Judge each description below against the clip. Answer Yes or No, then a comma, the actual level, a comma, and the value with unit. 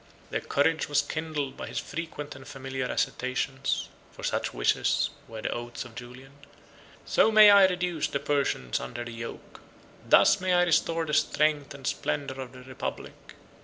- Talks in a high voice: No, medium, 140 Hz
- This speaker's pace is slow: No, average, 165 wpm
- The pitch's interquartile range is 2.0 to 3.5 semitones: No, average, 3.9 semitones